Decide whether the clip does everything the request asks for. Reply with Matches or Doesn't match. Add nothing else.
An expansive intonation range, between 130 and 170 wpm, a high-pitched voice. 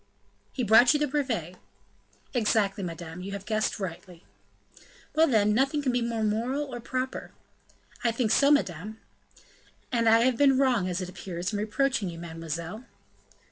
Matches